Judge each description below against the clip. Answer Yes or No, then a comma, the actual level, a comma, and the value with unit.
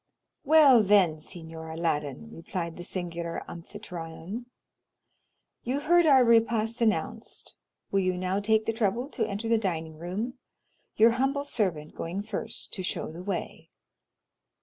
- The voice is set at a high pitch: Yes, high, 200 Hz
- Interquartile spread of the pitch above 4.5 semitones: Yes, wide, 5.6 semitones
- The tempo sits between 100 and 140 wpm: Yes, slow, 135 wpm